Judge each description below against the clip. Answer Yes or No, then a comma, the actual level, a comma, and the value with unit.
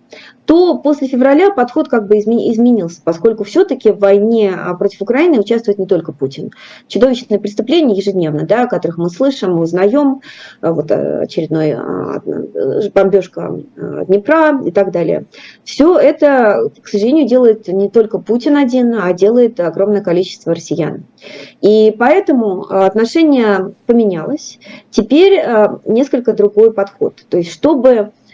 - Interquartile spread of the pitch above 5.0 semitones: Yes, wide, 5.5 semitones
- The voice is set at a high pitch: Yes, high, 220 Hz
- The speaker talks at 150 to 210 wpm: No, average, 125 wpm